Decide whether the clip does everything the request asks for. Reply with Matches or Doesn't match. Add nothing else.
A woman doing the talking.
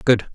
Doesn't match